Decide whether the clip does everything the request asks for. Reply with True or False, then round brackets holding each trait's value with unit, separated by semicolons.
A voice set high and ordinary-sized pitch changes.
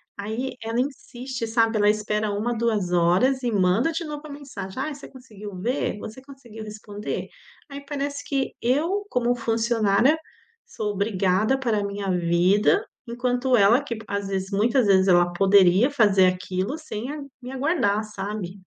True (220 Hz; 4.6 semitones)